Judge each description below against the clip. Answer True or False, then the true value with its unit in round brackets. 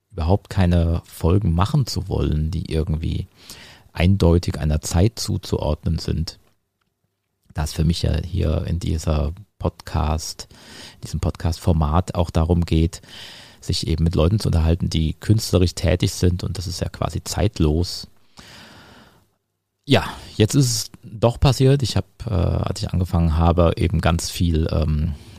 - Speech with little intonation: False (3.3 semitones)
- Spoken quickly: False (145 wpm)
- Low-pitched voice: True (90 Hz)